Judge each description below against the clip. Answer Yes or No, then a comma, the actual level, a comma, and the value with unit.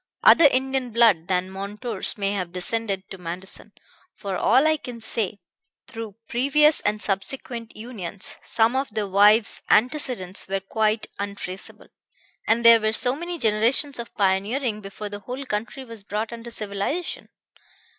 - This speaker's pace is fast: No, average, 145 wpm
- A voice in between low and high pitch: No, high, 220 Hz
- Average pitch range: Yes, average, 3.8 semitones